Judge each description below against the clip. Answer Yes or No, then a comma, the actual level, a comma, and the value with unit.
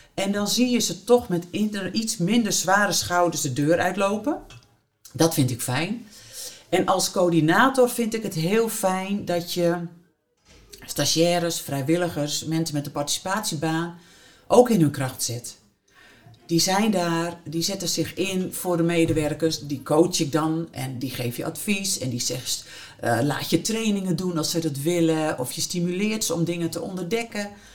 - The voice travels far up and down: No, average, 4.0 semitones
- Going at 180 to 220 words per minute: No, average, 170 wpm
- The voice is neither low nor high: Yes, medium, 170 Hz